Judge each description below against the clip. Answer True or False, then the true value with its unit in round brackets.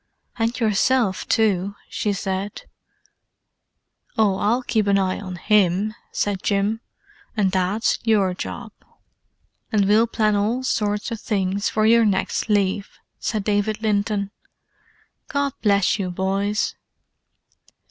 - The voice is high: True (205 Hz)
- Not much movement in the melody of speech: True (1.9 semitones)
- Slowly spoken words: True (120 wpm)